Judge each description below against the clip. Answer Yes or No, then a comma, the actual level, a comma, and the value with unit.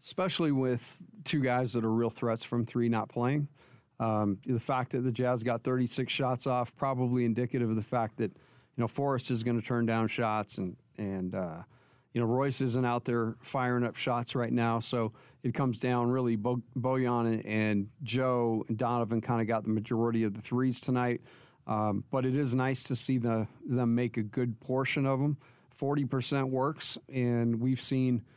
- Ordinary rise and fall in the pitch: No, narrow, 2.0 semitones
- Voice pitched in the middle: No, low, 125 Hz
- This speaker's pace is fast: No, average, 195 wpm